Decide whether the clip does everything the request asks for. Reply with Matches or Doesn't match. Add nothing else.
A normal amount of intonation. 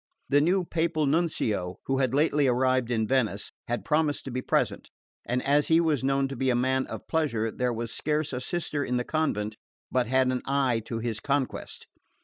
Matches